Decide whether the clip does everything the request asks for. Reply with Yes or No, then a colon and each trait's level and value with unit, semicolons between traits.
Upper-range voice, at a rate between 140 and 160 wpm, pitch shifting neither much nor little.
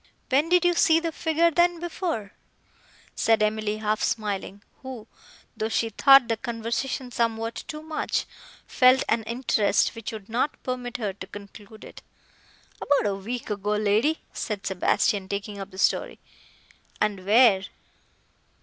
Yes: high, 225 Hz; average, 145 wpm; average, 4.2 semitones